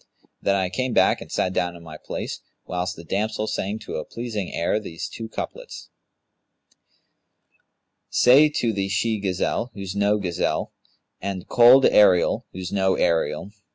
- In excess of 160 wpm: No, average, 155 wpm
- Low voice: Yes, low, 100 Hz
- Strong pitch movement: No, average, 3.3 semitones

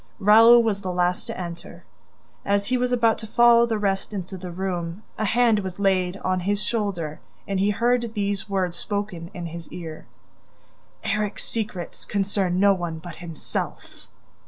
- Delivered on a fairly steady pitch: No, average, 3.3 semitones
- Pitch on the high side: Yes, high, 195 Hz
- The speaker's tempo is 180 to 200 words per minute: No, average, 165 wpm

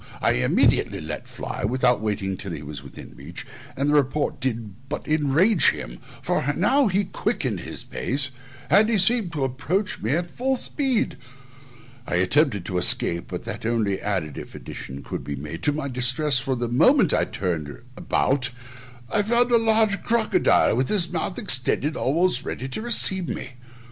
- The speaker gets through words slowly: No, average, 170 wpm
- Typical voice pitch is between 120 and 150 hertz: Yes, low, 135 Hz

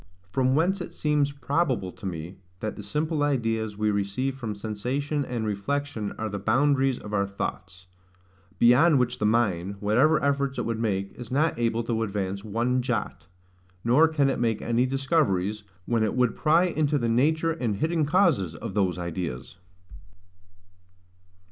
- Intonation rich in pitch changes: Yes, wide, 5.7 semitones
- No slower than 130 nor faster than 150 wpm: No, average, 160 wpm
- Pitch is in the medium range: No, low, 120 Hz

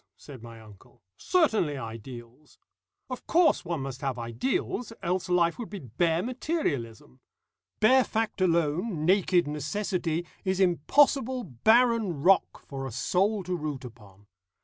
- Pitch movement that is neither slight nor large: No, wide, 8.2 semitones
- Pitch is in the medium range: Yes, medium, 170 Hz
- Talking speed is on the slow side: Yes, slow, 130 wpm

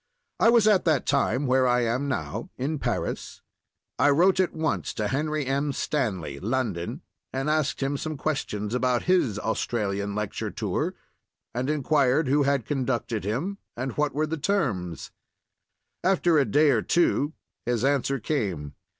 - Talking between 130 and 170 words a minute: Yes, average, 150 wpm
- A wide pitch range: No, average, 4.7 semitones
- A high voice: No, low, 135 Hz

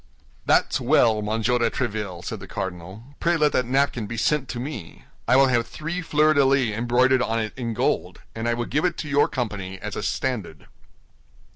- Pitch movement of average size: Yes, average, 4.2 semitones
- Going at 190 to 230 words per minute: Yes, average, 195 wpm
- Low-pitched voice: Yes, low, 120 Hz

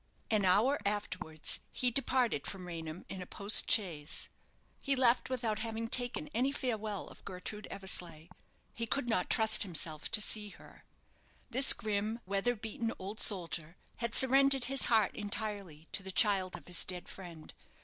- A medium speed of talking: Yes, average, 160 wpm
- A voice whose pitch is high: Yes, high, 210 Hz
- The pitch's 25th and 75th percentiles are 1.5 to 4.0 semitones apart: No, average, 4.4 semitones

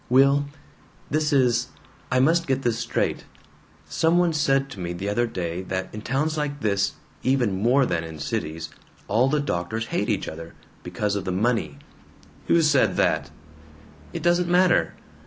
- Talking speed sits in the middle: Yes, average, 170 wpm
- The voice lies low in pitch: Yes, low, 120 Hz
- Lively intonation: Yes, wide, 7.2 semitones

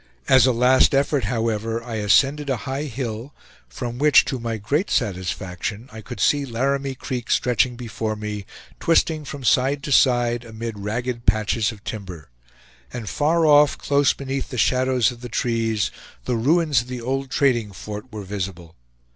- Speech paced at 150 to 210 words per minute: Yes, average, 165 wpm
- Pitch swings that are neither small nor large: Yes, average, 3.8 semitones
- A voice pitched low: Yes, low, 120 Hz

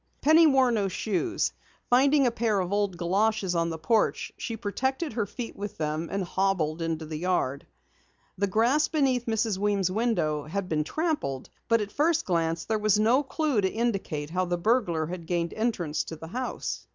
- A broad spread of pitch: Yes, wide, 5.8 semitones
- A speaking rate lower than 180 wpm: No, average, 185 wpm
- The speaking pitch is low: No, high, 200 Hz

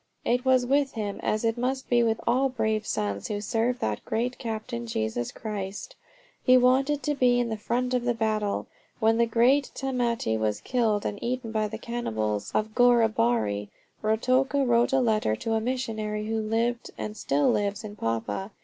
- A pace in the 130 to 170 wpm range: No, average, 180 wpm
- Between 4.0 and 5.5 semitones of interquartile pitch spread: No, average, 3.2 semitones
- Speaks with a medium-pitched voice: No, high, 225 Hz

